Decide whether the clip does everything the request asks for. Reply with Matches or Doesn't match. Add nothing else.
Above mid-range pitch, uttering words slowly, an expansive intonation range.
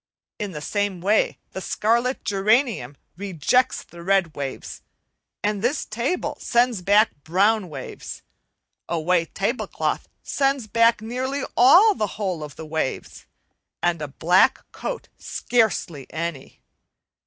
Matches